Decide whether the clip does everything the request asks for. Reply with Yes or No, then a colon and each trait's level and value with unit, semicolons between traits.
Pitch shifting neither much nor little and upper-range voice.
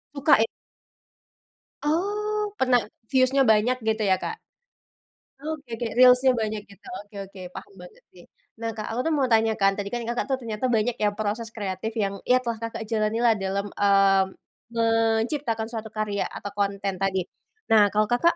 Yes: average, 3.5 semitones; high, 225 Hz